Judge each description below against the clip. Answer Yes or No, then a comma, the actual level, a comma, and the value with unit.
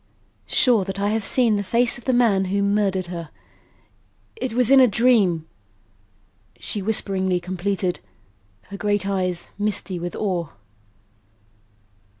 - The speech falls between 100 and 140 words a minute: Yes, slow, 135 wpm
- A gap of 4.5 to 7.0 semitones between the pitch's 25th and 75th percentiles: No, average, 3.1 semitones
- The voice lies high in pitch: Yes, high, 200 Hz